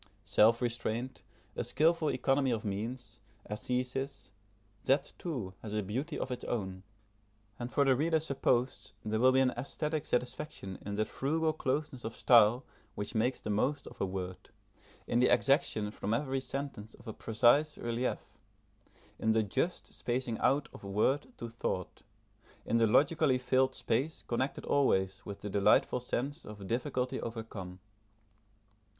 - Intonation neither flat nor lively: Yes, average, 4.0 semitones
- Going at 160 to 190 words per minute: No, average, 150 wpm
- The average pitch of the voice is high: No, low, 125 Hz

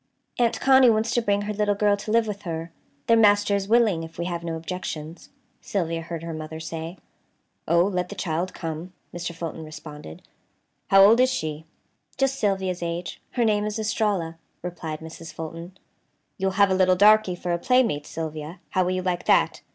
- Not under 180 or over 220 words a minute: Yes, average, 190 wpm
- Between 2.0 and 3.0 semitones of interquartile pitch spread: No, average, 4.0 semitones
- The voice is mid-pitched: Yes, medium, 180 Hz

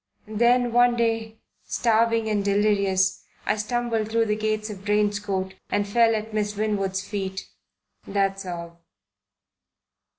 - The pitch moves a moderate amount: No, narrow, 2.3 semitones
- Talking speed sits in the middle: No, slow, 130 wpm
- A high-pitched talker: Yes, high, 210 Hz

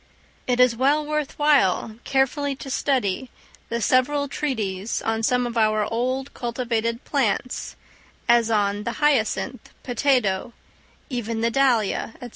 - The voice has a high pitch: Yes, high, 245 Hz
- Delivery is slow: Yes, slow, 130 wpm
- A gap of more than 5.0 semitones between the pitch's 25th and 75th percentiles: No, average, 3.3 semitones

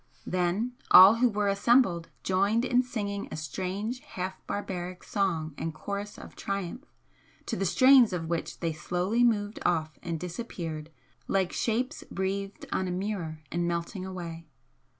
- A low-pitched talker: No, high, 190 Hz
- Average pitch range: Yes, average, 3.6 semitones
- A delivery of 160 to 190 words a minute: No, average, 150 wpm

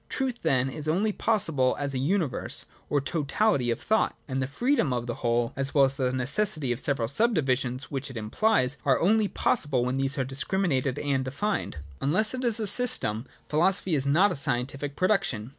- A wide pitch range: Yes, wide, 7.0 semitones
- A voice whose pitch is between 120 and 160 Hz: Yes, medium, 140 Hz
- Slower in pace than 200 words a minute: No, fast, 205 wpm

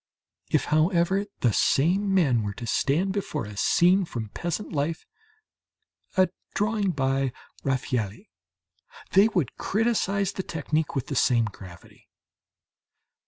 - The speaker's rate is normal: No, slow, 120 wpm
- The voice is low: No, medium, 160 Hz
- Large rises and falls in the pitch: Yes, wide, 6.9 semitones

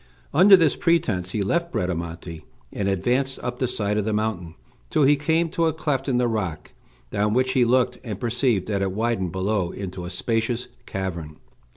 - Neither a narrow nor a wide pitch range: No, wide, 5.7 semitones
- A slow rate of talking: No, average, 190 wpm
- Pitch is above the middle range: No, low, 110 Hz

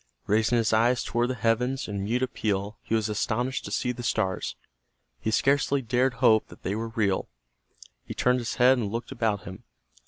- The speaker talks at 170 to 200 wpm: Yes, average, 190 wpm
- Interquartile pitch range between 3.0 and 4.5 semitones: No, narrow, 2.5 semitones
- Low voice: Yes, low, 115 Hz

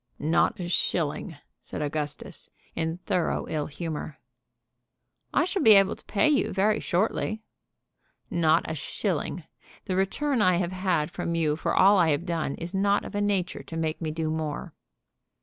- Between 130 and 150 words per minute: No, average, 170 wpm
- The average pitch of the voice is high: No, medium, 170 Hz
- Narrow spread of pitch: No, average, 3.8 semitones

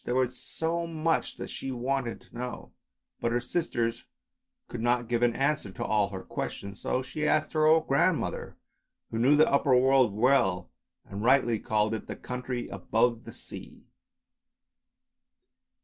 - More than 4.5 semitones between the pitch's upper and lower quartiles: No, average, 3.3 semitones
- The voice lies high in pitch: No, low, 125 Hz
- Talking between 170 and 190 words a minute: No, average, 160 wpm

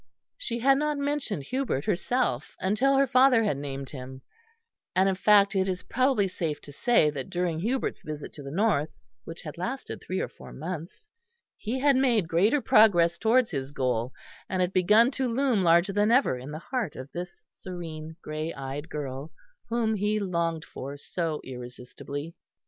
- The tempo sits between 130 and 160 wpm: No, average, 175 wpm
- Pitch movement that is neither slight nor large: No, wide, 7.4 semitones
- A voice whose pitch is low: No, medium, 180 Hz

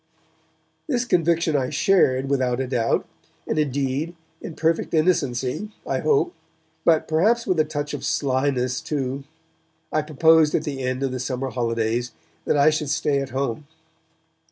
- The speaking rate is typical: Yes, average, 155 wpm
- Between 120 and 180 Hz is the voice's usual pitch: Yes, medium, 140 Hz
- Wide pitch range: No, average, 3.8 semitones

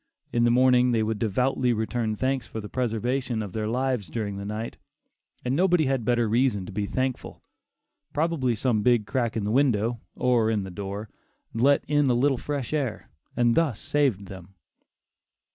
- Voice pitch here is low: Yes, low, 120 Hz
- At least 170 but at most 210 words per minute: Yes, average, 180 wpm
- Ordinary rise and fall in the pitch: Yes, average, 3.4 semitones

